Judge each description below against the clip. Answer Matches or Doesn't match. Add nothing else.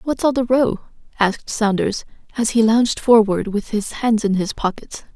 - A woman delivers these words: Matches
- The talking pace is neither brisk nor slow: Matches